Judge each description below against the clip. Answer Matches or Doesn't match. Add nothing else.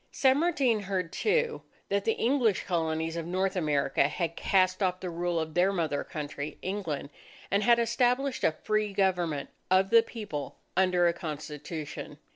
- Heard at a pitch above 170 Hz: Matches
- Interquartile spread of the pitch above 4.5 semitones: Matches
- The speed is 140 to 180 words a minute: Matches